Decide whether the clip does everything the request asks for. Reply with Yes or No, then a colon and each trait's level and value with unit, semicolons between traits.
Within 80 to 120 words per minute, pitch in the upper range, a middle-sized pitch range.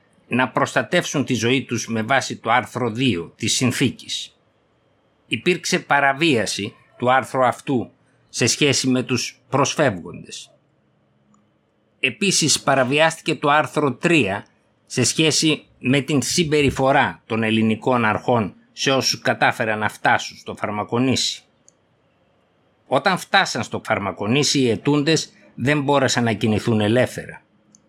No: slow, 115 wpm; low, 130 Hz; average, 4.0 semitones